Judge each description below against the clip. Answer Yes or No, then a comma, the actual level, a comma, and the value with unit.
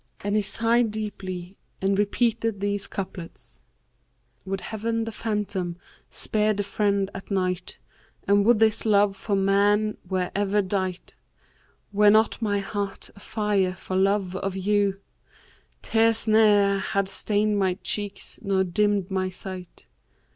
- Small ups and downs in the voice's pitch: Yes, narrow, 1.7 semitones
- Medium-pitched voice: No, high, 200 Hz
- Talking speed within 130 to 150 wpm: Yes, average, 140 wpm